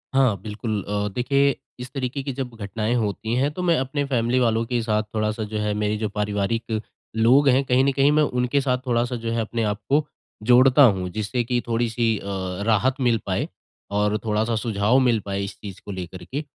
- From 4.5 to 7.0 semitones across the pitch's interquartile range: No, average, 3.3 semitones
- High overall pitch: No, low, 115 Hz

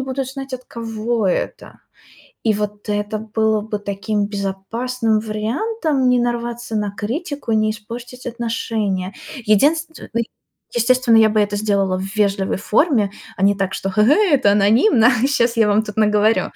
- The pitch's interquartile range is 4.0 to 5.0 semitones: No, average, 2.9 semitones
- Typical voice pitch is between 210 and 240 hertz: Yes, high, 220 Hz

